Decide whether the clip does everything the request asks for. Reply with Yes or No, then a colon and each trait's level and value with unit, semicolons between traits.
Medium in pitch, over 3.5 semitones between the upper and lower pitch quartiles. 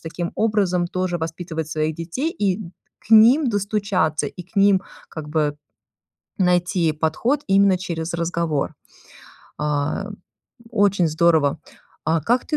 Yes: medium, 175 Hz; average, 3.9 semitones